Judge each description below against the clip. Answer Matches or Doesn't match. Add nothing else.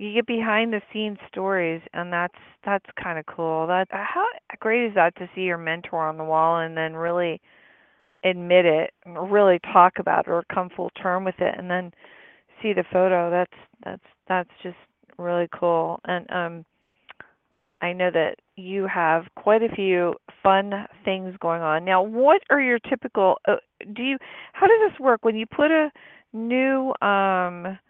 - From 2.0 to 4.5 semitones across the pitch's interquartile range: Matches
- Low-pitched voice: Doesn't match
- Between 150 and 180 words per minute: Matches